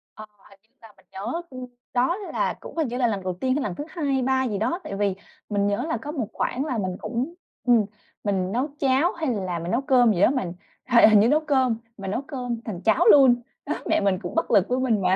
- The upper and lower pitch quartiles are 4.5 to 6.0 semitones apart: Yes, average, 4.8 semitones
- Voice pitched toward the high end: Yes, high, 235 Hz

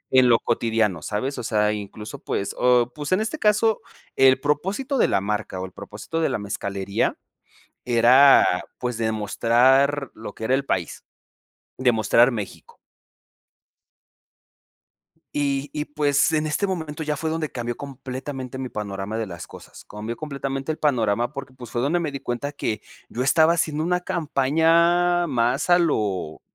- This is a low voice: Yes, low, 130 Hz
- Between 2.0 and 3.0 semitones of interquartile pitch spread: No, average, 5.3 semitones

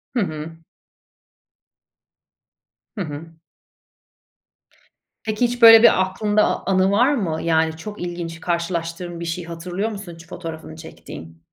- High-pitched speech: No, medium, 170 Hz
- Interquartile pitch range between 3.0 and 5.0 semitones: Yes, average, 3.6 semitones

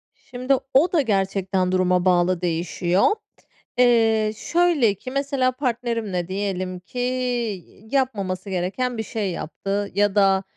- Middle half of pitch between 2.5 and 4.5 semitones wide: No, average, 5.1 semitones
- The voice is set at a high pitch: Yes, high, 205 Hz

